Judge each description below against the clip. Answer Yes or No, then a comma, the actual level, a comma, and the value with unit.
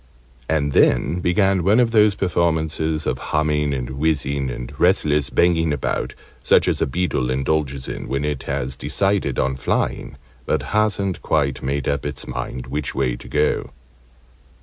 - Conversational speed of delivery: Yes, average, 155 wpm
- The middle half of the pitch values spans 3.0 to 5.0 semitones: Yes, average, 4.2 semitones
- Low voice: Yes, very low, 75 Hz